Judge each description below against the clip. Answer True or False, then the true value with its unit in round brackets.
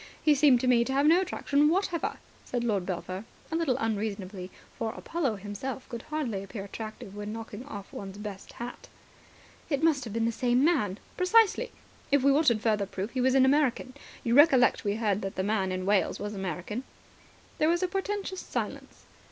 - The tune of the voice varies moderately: False (6.0 semitones)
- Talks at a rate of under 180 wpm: False (195 wpm)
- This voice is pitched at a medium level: False (235 Hz)